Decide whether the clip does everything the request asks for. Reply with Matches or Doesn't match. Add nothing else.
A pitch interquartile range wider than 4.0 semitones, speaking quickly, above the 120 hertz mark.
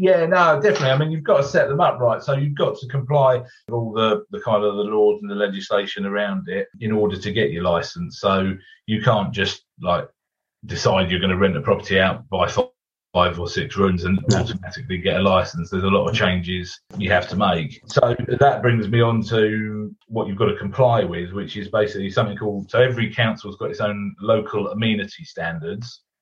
Doesn't match